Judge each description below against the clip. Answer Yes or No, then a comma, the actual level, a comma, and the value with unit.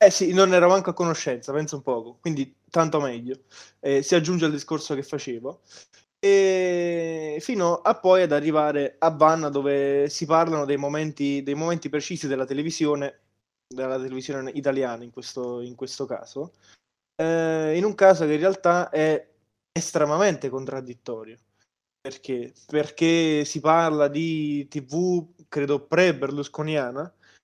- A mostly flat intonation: No, average, 3.2 semitones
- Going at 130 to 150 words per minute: Yes, average, 140 wpm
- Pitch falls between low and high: Yes, medium, 150 Hz